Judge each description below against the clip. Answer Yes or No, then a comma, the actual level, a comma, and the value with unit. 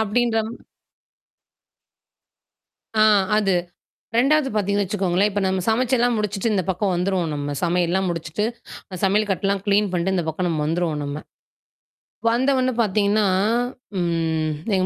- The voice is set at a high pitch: Yes, high, 195 Hz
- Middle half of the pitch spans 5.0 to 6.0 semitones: No, average, 3.5 semitones